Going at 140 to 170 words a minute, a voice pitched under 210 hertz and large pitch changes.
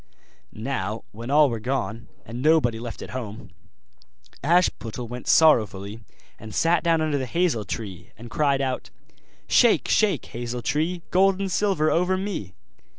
Yes: average, 150 wpm; low, 135 Hz; wide, 6.6 semitones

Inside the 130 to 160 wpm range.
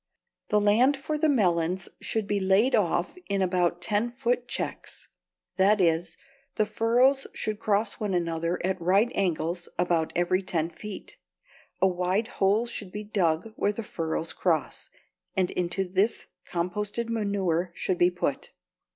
Yes: average, 150 wpm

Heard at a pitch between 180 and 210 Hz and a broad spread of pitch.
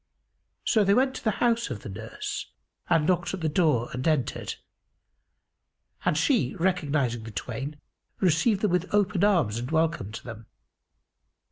No: medium, 160 Hz; wide, 7.7 semitones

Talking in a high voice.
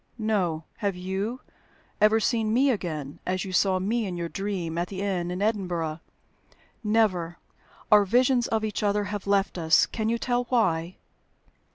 Yes: high, 200 Hz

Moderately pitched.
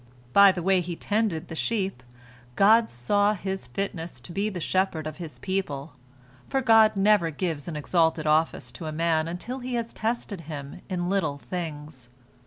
Yes: medium, 175 Hz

